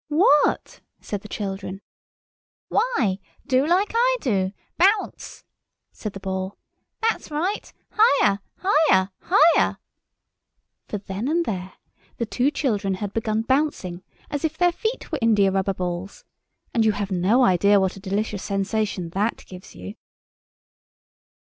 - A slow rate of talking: Yes, slow, 130 wpm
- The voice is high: Yes, high, 210 Hz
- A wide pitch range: Yes, wide, 7.7 semitones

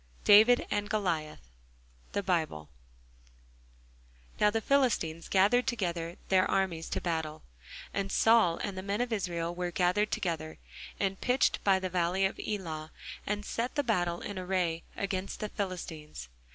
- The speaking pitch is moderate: Yes, medium, 180 Hz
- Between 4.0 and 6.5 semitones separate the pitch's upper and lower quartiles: Yes, average, 4.5 semitones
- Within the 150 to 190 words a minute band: No, average, 140 wpm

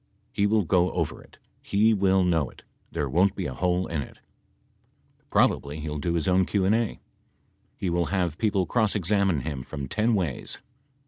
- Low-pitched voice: Yes, very low, 90 Hz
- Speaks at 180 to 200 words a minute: Yes, average, 190 wpm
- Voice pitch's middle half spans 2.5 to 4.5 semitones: Yes, average, 4.1 semitones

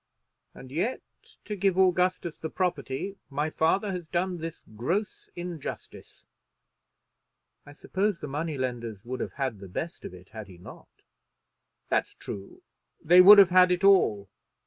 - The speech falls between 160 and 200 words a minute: No, average, 150 wpm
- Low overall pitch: No, medium, 165 Hz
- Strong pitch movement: Yes, wide, 6.1 semitones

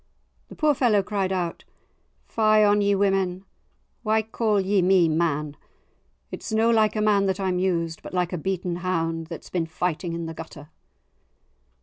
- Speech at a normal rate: Yes, average, 165 wpm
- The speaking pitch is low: No, medium, 185 Hz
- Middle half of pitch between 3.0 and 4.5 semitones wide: Yes, average, 3.6 semitones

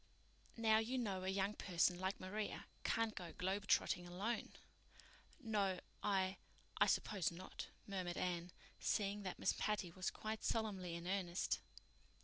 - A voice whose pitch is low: No, high, 190 Hz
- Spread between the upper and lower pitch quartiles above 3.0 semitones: No, average, 2.7 semitones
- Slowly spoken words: Yes, slow, 130 wpm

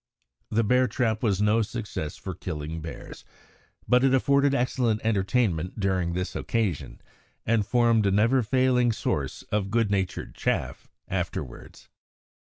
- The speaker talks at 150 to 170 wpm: No, slow, 135 wpm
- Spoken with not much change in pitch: No, average, 4.3 semitones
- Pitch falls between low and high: No, low, 110 Hz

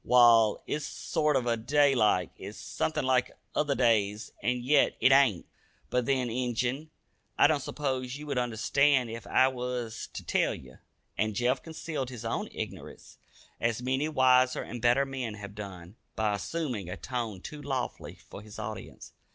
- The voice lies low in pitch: Yes, low, 125 Hz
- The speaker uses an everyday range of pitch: Yes, average, 3.6 semitones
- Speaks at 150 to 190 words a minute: Yes, average, 165 wpm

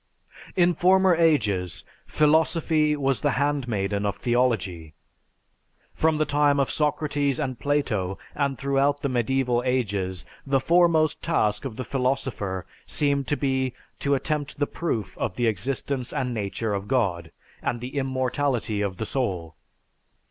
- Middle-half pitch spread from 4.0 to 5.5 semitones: Yes, average, 5.1 semitones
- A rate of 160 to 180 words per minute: No, average, 140 wpm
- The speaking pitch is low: Yes, low, 130 Hz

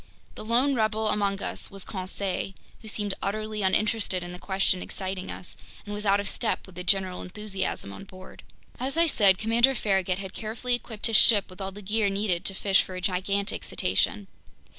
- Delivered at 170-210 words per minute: Yes, average, 195 wpm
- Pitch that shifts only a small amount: Yes, narrow, 2.3 semitones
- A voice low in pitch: No, high, 200 Hz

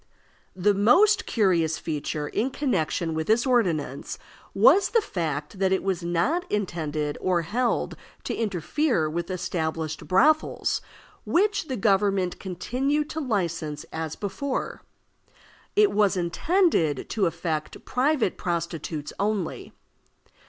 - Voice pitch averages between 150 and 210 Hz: Yes, high, 190 Hz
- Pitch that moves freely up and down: Yes, wide, 7.5 semitones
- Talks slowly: Yes, slow, 115 wpm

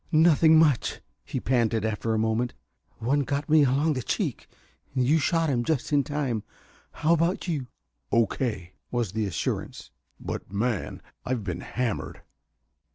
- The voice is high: No, low, 125 Hz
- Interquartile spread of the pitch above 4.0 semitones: Yes, average, 5.1 semitones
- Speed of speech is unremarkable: Yes, average, 145 wpm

